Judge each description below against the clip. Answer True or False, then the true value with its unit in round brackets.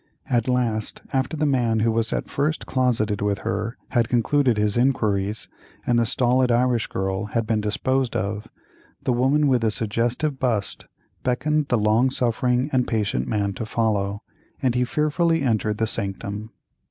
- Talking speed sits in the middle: True (165 wpm)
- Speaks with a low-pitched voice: True (115 Hz)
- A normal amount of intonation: True (3.3 semitones)